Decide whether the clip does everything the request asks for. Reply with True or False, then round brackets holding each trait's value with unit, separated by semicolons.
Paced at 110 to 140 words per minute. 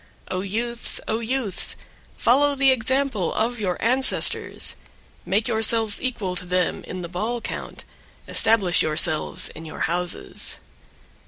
True (135 wpm)